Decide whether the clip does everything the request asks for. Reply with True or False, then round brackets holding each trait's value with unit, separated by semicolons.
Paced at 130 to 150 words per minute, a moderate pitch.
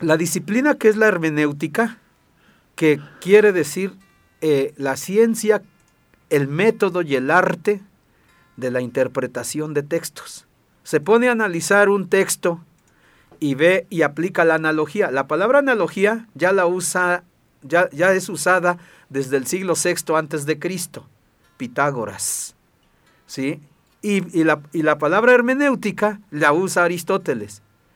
True (135 wpm; 175 Hz)